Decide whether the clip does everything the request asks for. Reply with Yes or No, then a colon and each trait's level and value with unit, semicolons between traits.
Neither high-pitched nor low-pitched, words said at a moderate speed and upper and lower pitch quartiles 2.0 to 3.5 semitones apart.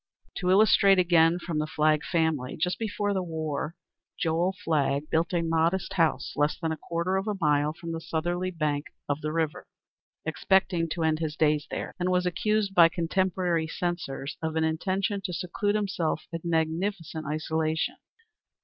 Yes: medium, 165 Hz; average, 165 wpm; narrow, 2.6 semitones